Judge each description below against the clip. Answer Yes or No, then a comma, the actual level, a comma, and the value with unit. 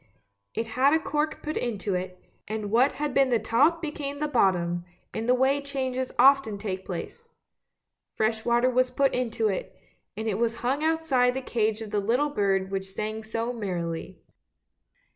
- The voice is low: No, high, 235 Hz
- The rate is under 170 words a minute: No, average, 175 wpm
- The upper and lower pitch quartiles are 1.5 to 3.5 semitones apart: No, average, 4.6 semitones